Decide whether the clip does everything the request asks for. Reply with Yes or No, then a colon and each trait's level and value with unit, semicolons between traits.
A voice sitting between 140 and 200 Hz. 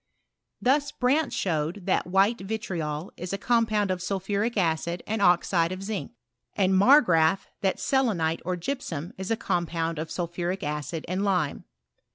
Yes: medium, 185 Hz